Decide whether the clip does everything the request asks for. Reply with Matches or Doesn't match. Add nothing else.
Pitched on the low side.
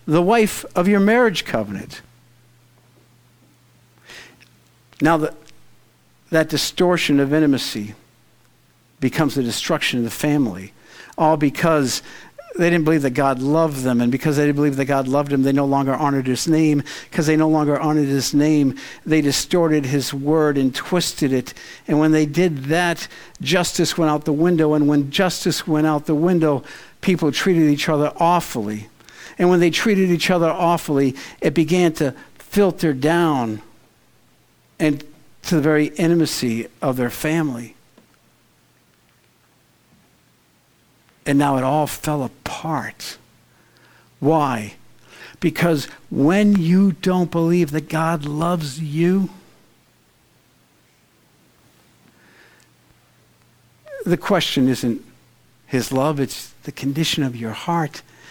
Doesn't match